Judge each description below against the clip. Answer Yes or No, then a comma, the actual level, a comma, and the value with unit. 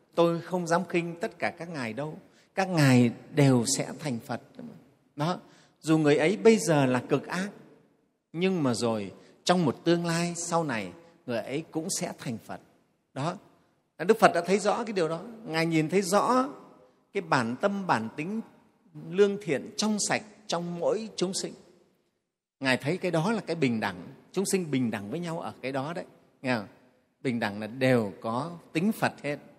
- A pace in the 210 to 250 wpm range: No, average, 190 wpm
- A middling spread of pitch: No, wide, 6.1 semitones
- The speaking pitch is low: No, medium, 165 Hz